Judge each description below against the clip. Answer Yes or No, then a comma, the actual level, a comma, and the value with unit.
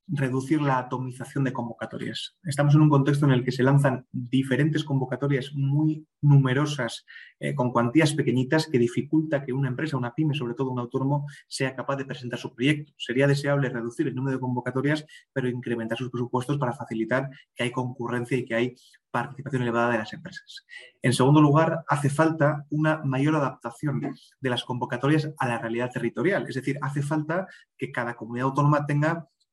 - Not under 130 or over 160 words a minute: No, average, 175 wpm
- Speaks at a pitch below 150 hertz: Yes, low, 135 Hz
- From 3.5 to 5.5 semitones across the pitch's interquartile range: No, average, 2.9 semitones